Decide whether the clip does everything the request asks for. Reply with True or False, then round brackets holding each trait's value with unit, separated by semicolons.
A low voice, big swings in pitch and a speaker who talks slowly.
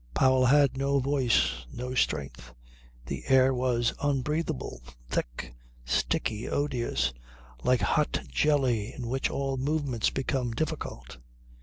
False (130 Hz; 3.3 semitones; 115 wpm)